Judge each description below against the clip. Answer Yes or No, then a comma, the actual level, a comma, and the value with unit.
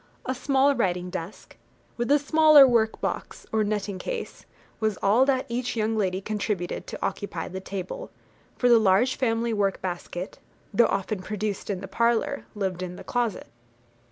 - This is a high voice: Yes, high, 215 Hz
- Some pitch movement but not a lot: Yes, average, 4.3 semitones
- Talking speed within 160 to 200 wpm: Yes, average, 165 wpm